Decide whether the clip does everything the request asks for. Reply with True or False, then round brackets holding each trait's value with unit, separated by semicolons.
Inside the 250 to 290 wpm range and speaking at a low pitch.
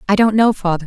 False (280 wpm; 205 Hz)